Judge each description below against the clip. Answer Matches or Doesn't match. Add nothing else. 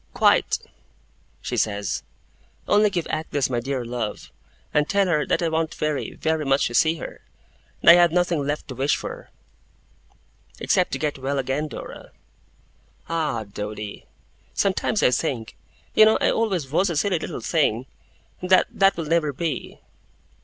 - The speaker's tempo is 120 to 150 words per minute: Doesn't match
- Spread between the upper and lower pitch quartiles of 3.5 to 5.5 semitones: Matches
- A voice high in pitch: Doesn't match